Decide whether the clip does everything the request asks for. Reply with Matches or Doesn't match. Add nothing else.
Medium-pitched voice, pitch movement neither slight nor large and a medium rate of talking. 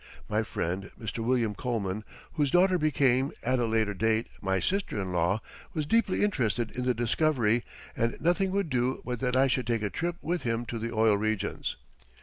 Doesn't match